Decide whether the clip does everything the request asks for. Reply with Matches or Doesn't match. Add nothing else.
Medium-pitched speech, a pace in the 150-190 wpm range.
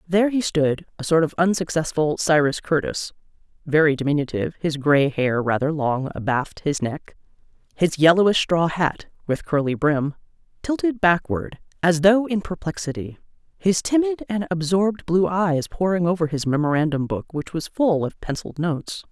Matches